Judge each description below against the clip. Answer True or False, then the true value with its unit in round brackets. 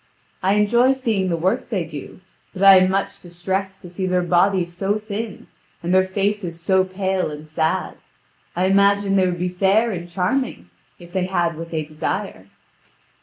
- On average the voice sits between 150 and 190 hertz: True (185 Hz)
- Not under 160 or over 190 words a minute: True (175 wpm)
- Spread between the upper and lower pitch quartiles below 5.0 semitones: True (2.4 semitones)